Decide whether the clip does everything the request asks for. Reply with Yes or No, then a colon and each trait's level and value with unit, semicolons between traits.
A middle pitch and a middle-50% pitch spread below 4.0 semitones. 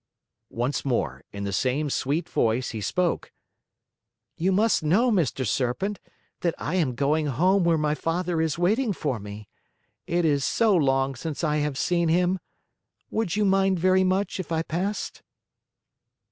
No: medium, 165 Hz; wide, 5.5 semitones